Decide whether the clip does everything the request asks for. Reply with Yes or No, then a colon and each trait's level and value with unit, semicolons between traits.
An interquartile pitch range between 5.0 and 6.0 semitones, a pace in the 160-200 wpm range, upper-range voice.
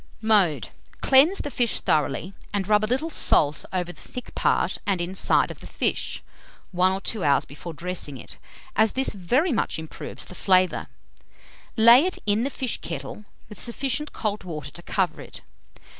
Yes: wide, 5.5 semitones; average, 175 wpm; high, 200 Hz